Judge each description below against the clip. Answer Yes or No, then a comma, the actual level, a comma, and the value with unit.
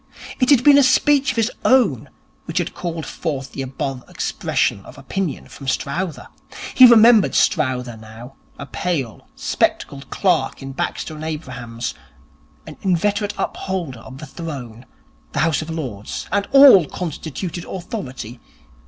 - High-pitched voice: No, medium, 155 Hz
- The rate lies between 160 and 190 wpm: No, average, 145 wpm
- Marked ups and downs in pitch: Yes, wide, 7.3 semitones